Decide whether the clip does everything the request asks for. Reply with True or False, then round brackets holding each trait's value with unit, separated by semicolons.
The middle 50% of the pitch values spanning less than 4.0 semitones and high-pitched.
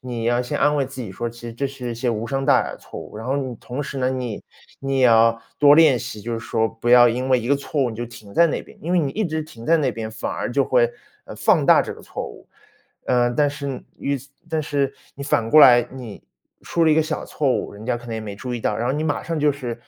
False (3.3 semitones; 125 Hz)